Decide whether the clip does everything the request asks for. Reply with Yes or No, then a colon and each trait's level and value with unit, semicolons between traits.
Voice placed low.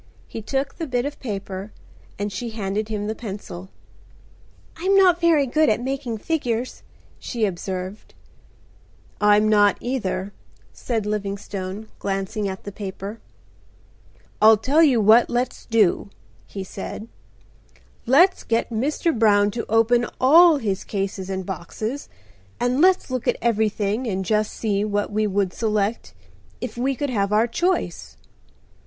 No: high, 220 Hz